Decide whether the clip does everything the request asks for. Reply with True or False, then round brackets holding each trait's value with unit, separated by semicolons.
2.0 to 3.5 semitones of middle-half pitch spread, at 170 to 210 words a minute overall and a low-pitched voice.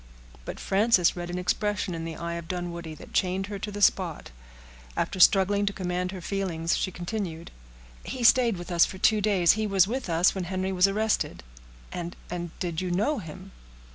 False (2.7 semitones; 180 wpm; 185 Hz)